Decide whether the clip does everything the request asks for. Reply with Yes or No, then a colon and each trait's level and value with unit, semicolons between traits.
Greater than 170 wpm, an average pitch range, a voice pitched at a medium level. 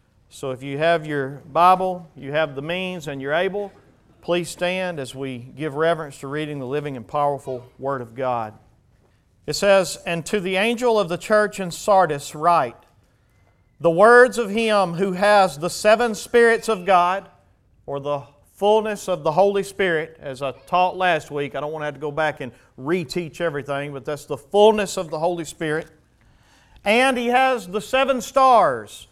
No: average, 180 wpm; wide, 5.7 semitones; medium, 165 Hz